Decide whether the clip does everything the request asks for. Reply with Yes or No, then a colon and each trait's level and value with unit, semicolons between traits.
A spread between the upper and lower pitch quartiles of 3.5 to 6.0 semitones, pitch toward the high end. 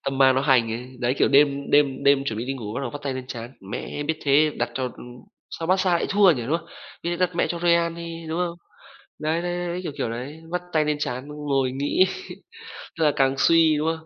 No: average, 4.0 semitones; medium, 145 Hz